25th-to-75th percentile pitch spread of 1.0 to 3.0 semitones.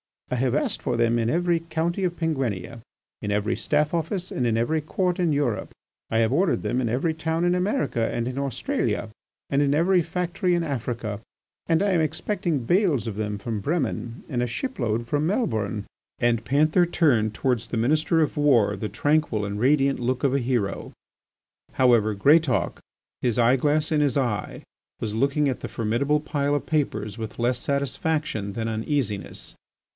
No: wide, 5.6 semitones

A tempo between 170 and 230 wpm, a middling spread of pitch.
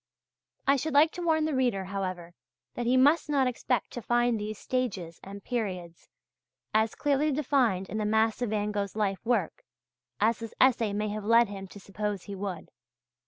Yes: average, 185 wpm; average, 4.3 semitones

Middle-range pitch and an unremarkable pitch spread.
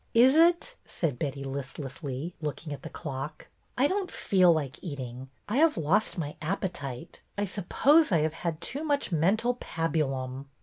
No: medium, 165 Hz; wide, 7.7 semitones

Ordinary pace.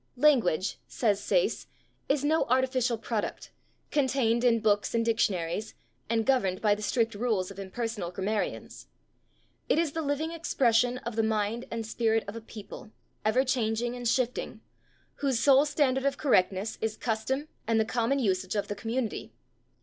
Yes: average, 155 wpm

